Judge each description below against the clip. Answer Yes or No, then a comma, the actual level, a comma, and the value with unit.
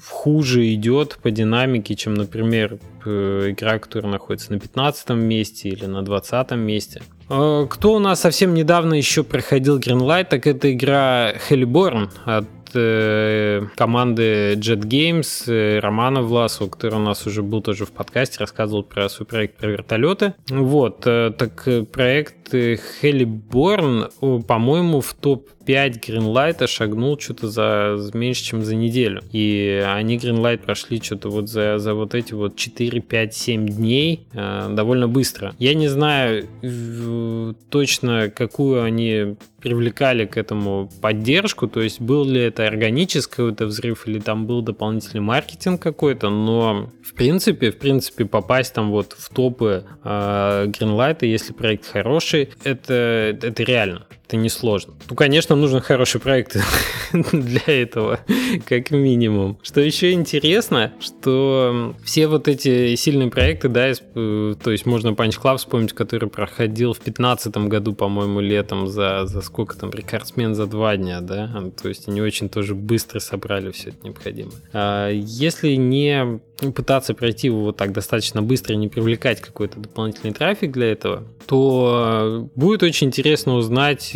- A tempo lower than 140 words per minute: No, average, 145 wpm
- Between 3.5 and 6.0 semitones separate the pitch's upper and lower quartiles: Yes, average, 3.9 semitones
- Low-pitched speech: Yes, low, 115 Hz